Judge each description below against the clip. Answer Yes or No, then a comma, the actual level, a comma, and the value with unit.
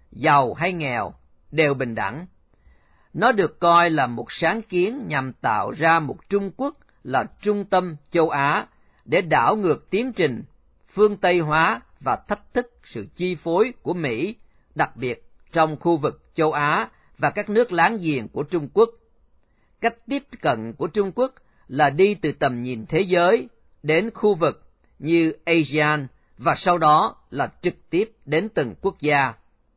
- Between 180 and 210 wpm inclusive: No, slow, 165 wpm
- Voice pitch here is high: No, medium, 165 Hz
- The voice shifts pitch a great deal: Yes, wide, 6.2 semitones